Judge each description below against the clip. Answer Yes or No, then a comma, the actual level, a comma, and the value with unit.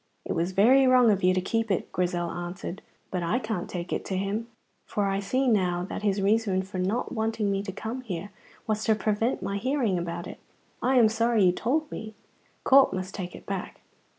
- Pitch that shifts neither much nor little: Yes, average, 3.6 semitones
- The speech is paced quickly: Yes, fast, 210 wpm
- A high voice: Yes, high, 200 Hz